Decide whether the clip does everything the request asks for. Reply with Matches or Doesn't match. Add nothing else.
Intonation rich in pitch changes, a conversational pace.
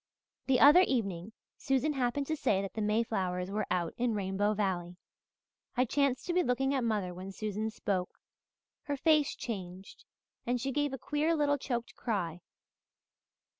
Matches